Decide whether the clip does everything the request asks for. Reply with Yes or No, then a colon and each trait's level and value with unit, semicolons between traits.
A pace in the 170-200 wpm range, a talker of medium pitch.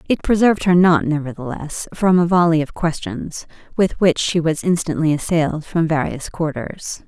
No: average, 160 wpm; medium, 160 Hz